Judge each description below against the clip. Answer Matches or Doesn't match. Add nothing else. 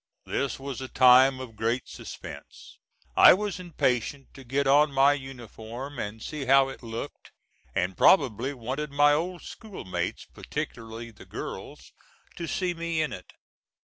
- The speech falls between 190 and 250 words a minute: Doesn't match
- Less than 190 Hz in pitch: Matches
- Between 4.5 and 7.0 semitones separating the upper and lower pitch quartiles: Doesn't match